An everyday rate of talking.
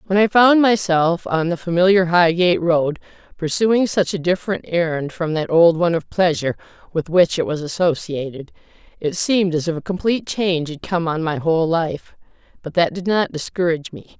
Yes: average, 185 wpm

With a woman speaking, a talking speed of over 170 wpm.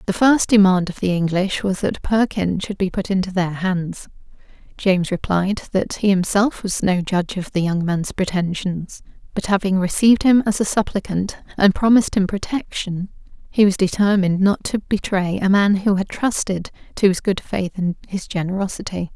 Yes: female; average, 180 wpm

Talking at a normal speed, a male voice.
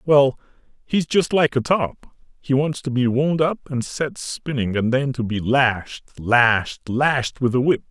Yes: average, 190 wpm; male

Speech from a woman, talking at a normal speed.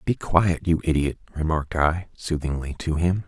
No: male; average, 165 wpm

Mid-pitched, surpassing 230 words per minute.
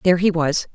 Yes: medium, 170 Hz; fast, 240 wpm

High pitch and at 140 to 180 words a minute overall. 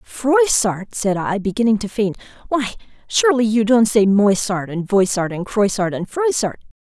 Yes: high, 215 Hz; average, 160 wpm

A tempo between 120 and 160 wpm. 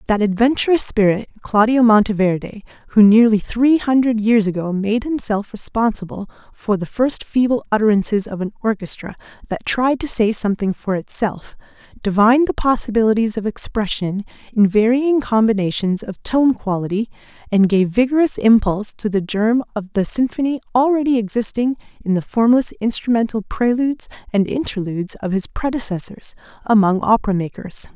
Yes: average, 140 wpm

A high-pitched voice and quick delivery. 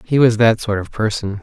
No: low, 110 Hz; fast, 255 wpm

